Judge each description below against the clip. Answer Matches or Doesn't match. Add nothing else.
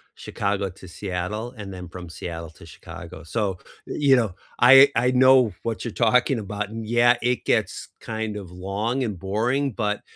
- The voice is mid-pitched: Doesn't match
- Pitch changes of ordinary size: Matches